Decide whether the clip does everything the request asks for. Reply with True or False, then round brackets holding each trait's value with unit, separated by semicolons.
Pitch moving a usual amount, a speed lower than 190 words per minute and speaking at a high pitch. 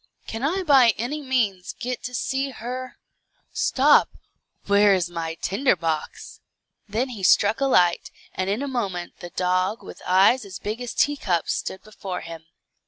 False (5.9 semitones; 165 wpm; 210 Hz)